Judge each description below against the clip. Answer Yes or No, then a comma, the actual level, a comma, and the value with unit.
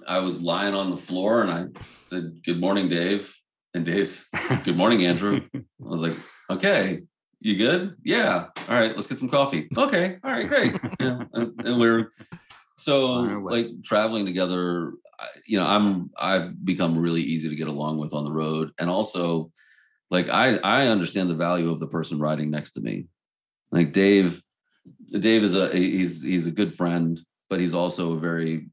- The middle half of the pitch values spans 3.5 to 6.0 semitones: Yes, average, 3.9 semitones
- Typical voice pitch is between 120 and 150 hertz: No, very low, 90 Hz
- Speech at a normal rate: Yes, average, 180 wpm